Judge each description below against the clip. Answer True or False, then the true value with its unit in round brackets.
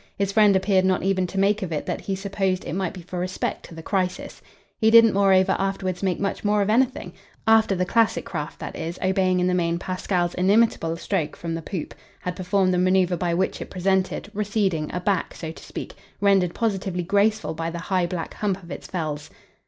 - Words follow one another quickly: True (215 wpm)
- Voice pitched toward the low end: False (185 Hz)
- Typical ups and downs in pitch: False (2.1 semitones)